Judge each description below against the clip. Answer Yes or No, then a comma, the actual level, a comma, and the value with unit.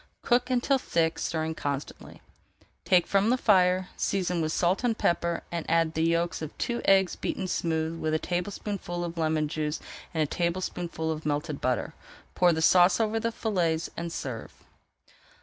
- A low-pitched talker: No, medium, 170 Hz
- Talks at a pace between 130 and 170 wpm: Yes, average, 165 wpm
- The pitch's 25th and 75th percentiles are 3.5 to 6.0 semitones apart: No, average, 3.0 semitones